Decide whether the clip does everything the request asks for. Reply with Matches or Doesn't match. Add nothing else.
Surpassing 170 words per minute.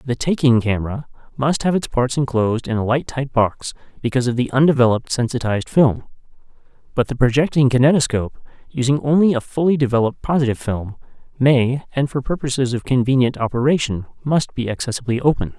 Doesn't match